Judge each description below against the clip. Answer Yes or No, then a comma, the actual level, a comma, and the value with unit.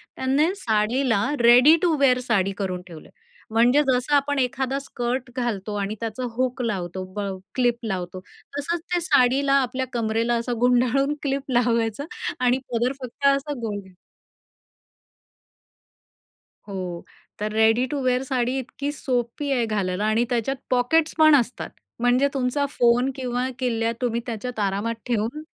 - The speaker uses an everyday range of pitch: Yes, average, 3.1 semitones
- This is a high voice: Yes, high, 245 Hz